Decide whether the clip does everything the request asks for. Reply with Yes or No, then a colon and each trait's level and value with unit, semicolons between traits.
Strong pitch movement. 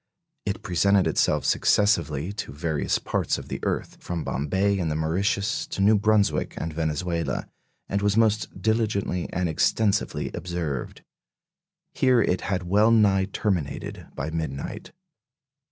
No: average, 4.0 semitones